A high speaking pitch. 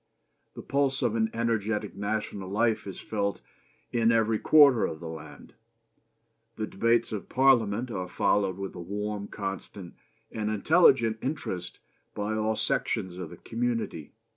No: low, 110 Hz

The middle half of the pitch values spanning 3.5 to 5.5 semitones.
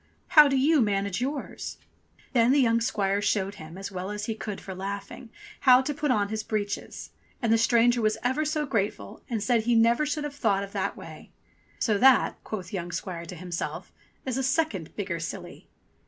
Yes: average, 4.6 semitones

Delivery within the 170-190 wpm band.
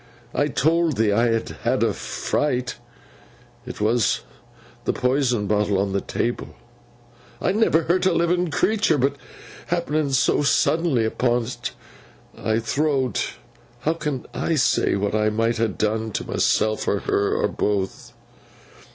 No: average, 140 wpm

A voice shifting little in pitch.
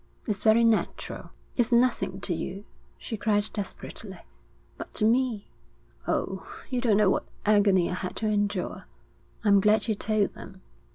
Yes: narrow, 2.3 semitones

